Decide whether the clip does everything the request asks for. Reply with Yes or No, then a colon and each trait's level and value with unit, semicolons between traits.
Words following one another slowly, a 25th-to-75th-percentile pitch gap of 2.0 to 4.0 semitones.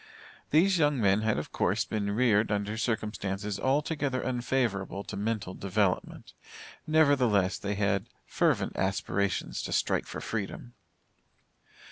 No: slow, 120 wpm; average, 4.4 semitones